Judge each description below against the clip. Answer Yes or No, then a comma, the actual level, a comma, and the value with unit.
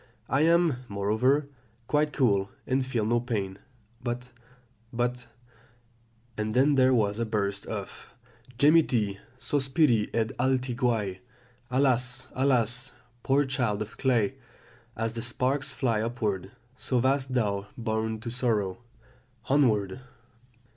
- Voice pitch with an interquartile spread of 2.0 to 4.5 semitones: Yes, average, 3.4 semitones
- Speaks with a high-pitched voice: No, low, 120 Hz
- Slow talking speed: Yes, slow, 120 wpm